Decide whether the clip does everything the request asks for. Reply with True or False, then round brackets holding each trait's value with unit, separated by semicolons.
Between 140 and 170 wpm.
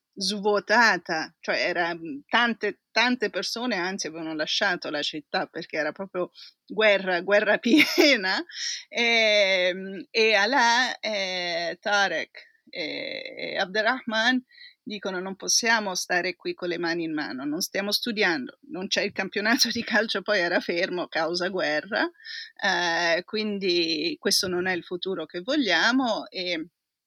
False (125 wpm)